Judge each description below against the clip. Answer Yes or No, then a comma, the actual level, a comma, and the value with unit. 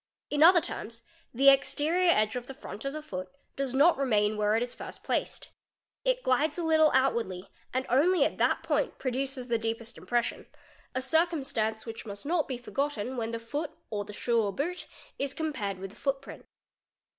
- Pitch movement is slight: No, average, 4.6 semitones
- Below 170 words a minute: No, average, 185 wpm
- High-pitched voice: Yes, very high, 260 Hz